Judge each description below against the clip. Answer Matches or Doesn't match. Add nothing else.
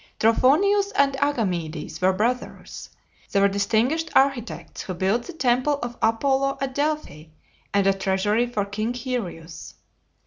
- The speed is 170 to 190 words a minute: Doesn't match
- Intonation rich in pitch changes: Matches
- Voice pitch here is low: Doesn't match